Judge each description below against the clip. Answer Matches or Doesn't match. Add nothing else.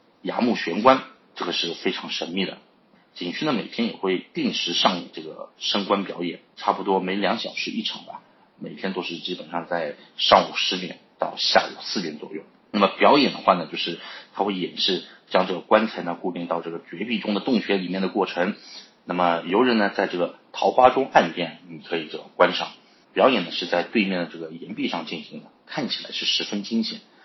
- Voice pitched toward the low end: Matches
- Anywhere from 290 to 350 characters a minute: Matches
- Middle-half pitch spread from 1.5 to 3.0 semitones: Doesn't match